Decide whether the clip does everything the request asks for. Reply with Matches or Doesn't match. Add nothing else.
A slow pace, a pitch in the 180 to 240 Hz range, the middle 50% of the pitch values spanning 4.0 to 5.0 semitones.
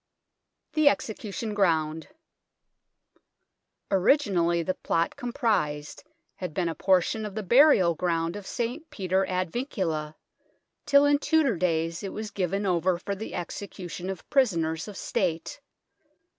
Matches